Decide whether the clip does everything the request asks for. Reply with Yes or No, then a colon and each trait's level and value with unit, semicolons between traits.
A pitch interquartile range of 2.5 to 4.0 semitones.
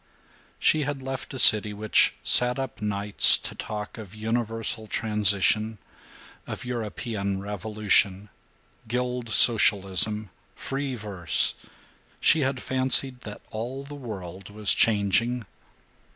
Yes: average, 3.3 semitones